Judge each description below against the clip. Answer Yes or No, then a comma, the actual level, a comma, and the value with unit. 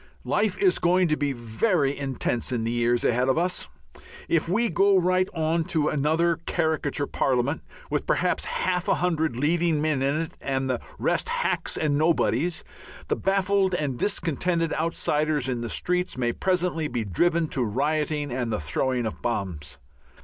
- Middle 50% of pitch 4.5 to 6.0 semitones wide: Yes, average, 5.2 semitones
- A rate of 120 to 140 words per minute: No, average, 165 wpm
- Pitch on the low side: No, medium, 155 Hz